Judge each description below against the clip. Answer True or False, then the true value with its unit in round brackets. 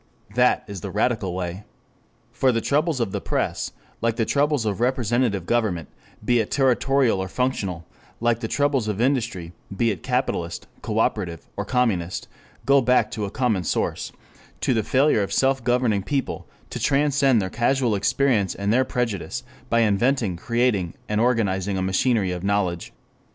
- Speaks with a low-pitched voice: True (115 Hz)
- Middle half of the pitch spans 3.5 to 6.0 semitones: True (4.6 semitones)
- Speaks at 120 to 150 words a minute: False (160 wpm)